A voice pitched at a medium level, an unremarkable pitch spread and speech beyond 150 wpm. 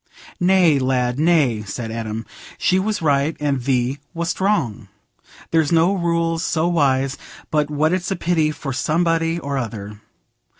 No: medium, 150 Hz; average, 4.6 semitones; average, 145 wpm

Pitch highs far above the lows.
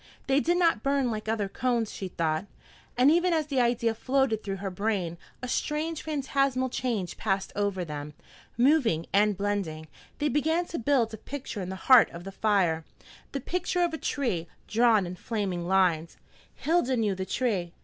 Yes: wide, 6.4 semitones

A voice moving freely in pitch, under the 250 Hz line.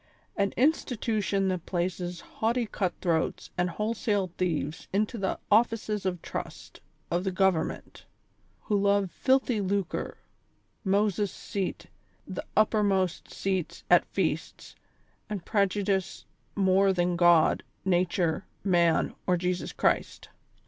No: narrow, 2.6 semitones; high, 190 Hz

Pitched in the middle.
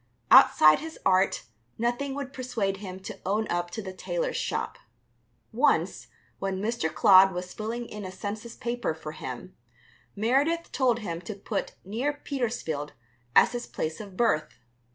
No: high, 215 Hz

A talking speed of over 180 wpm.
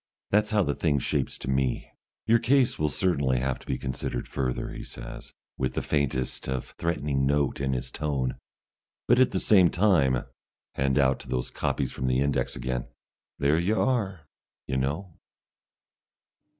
No: average, 165 wpm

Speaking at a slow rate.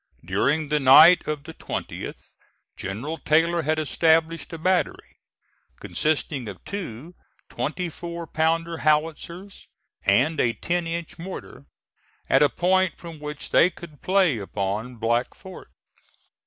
Yes: slow, 130 wpm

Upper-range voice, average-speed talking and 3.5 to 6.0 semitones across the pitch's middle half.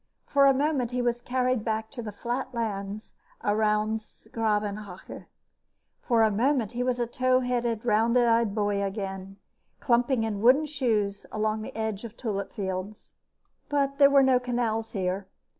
No: high, 225 Hz; average, 165 wpm; average, 3.0 semitones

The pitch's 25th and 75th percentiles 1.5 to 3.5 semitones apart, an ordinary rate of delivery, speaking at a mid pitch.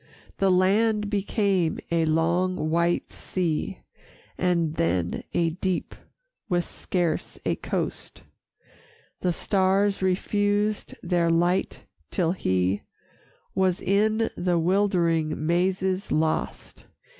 No: average, 2.8 semitones; slow, 100 wpm; medium, 180 Hz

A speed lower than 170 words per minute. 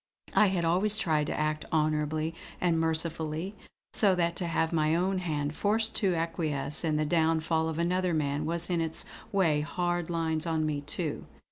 No: average, 175 wpm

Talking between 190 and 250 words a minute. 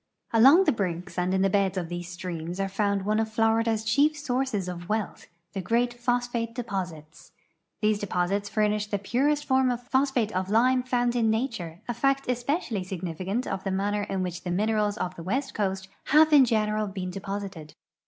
Yes: average, 195 wpm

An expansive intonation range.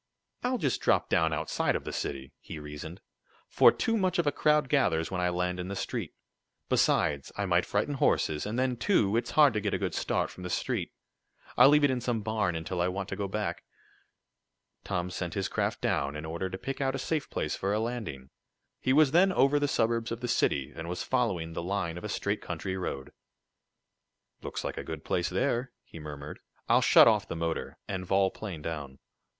Yes: wide, 6.9 semitones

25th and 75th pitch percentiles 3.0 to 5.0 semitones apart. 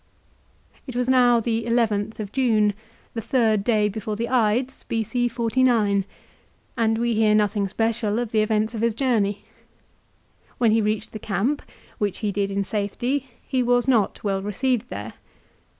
No: narrow, 2.6 semitones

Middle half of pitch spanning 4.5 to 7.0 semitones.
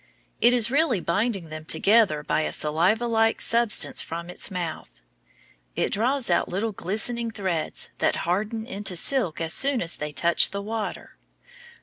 Yes: wide, 5.4 semitones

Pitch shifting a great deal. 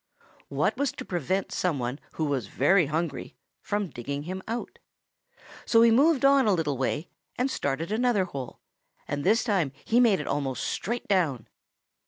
Yes: wide, 8.0 semitones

